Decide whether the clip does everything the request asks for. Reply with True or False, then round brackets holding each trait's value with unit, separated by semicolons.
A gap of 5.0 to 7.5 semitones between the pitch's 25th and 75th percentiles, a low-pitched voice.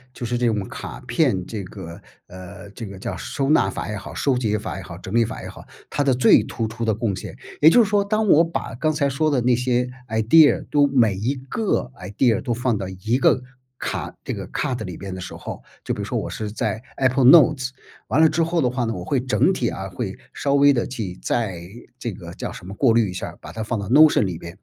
True (5.6 semitones; 120 Hz)